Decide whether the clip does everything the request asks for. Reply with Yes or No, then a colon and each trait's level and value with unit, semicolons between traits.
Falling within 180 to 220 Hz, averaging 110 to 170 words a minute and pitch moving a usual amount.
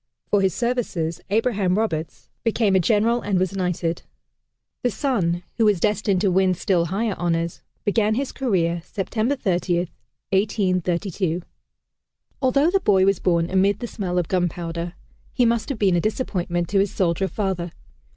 Yes: high, 190 Hz; average, 155 wpm; average, 3.7 semitones